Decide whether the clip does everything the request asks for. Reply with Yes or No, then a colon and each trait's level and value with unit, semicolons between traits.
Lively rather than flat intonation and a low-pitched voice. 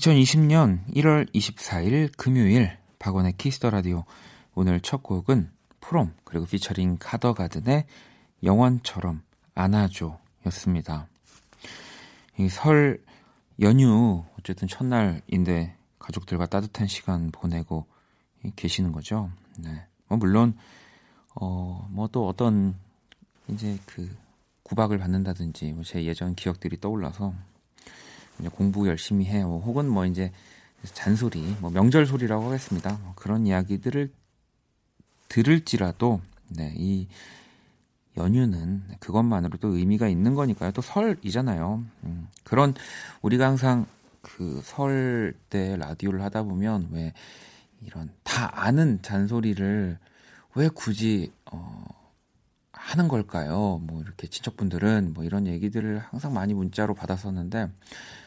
No: average, 4.3 semitones; low, 100 Hz